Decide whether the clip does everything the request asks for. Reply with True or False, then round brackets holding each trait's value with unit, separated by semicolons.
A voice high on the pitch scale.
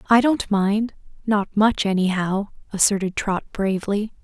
True (205 Hz)